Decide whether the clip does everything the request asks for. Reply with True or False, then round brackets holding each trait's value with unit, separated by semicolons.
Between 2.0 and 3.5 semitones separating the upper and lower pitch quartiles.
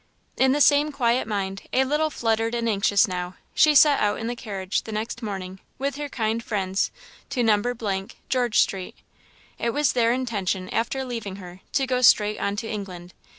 False (4.3 semitones)